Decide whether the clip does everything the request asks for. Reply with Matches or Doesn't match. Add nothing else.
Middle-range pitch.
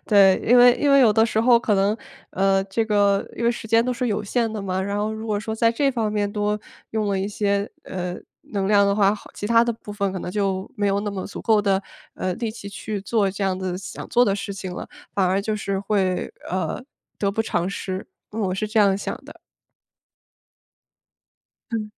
Doesn't match